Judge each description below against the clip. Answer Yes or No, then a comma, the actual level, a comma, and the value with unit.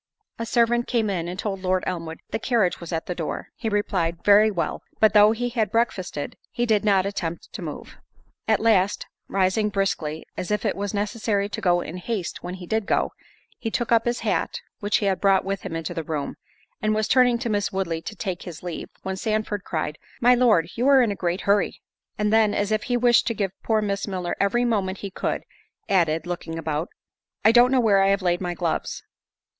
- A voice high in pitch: Yes, high, 200 Hz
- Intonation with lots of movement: No, average, 3.7 semitones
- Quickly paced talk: Yes, fast, 220 wpm